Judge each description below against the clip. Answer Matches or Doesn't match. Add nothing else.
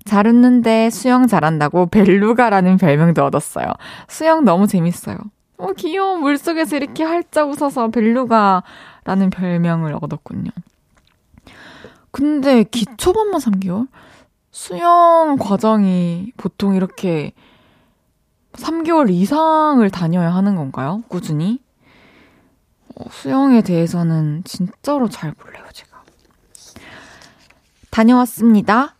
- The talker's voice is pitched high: Matches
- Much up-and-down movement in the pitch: Matches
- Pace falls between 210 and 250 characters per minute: Matches